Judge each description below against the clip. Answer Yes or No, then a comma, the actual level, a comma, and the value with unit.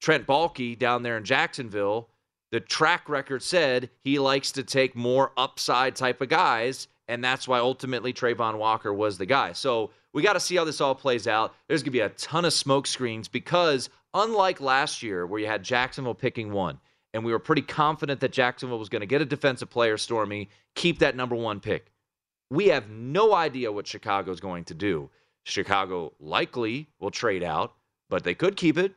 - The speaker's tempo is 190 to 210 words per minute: Yes, average, 200 wpm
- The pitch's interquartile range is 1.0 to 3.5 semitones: No, average, 3.9 semitones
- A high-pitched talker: No, low, 125 Hz